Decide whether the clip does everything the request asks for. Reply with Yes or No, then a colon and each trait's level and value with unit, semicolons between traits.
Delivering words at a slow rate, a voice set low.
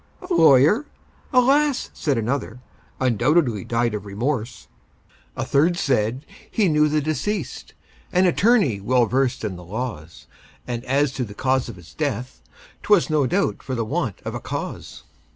No: average, 155 wpm; low, 130 Hz